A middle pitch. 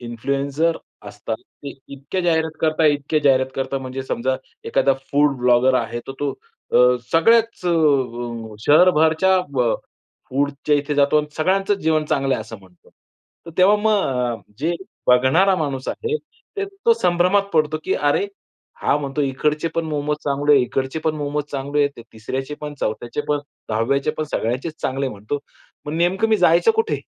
Yes: medium, 145 Hz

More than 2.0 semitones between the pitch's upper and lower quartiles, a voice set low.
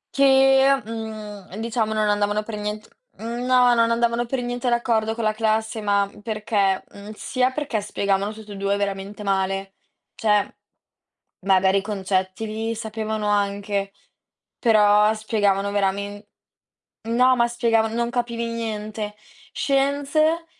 No: narrow, 2.6 semitones; high, 215 Hz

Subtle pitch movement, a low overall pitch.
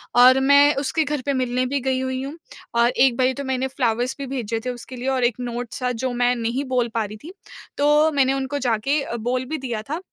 No: narrow, 2.3 semitones; very high, 255 Hz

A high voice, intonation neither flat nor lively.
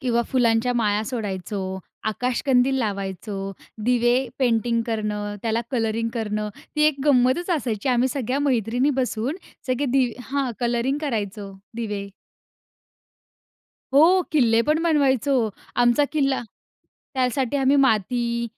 Yes: high, 240 Hz; average, 3.6 semitones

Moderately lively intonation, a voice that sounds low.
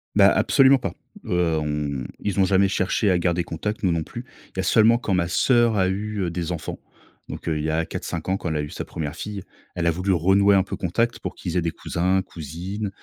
Yes: average, 3.3 semitones; very low, 90 Hz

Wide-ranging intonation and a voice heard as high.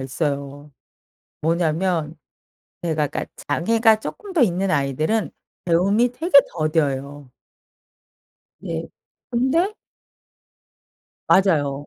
No: wide, 7.2 semitones; medium, 165 Hz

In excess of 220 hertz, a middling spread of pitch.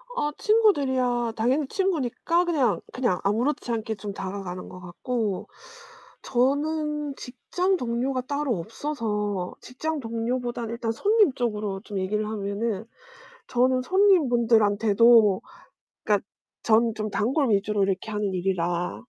Yes: high, 235 Hz; average, 4.8 semitones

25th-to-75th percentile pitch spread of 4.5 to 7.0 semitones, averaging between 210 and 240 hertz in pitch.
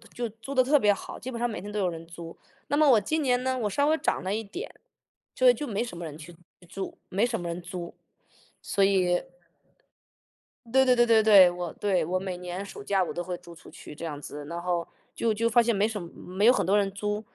No: average, 4.9 semitones; high, 200 Hz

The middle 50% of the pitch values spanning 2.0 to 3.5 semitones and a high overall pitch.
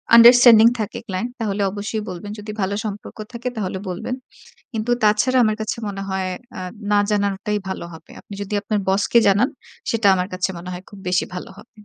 Yes: narrow, 2.6 semitones; high, 205 Hz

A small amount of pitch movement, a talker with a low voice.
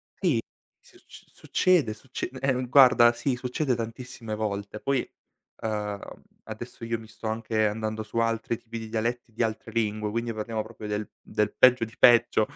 Yes: narrow, 2.1 semitones; low, 115 Hz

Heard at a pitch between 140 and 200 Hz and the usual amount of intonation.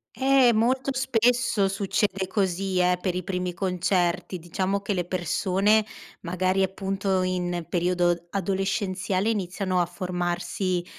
No: medium, 185 Hz; narrow, 1.9 semitones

